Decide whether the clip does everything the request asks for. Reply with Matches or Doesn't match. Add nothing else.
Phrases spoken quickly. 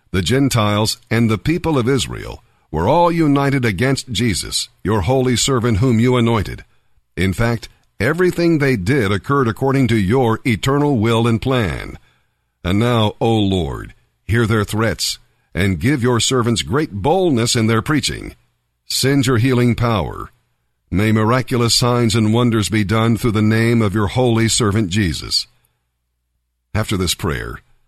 Doesn't match